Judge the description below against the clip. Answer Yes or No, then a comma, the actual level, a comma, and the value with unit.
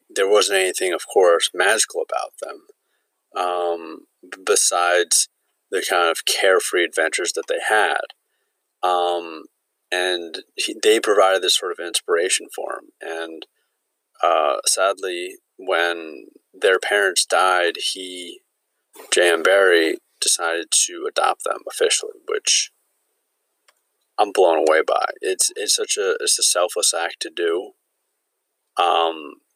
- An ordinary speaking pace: No, slow, 120 wpm